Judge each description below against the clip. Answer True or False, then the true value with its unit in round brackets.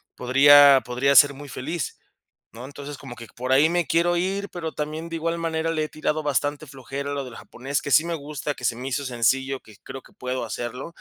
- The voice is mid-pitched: True (145 Hz)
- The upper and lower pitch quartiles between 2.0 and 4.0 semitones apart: True (3.5 semitones)